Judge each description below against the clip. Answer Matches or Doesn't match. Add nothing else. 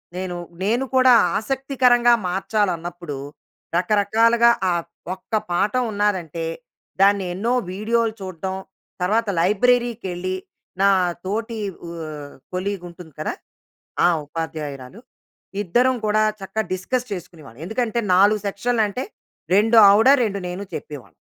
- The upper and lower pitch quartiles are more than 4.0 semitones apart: Matches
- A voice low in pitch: Doesn't match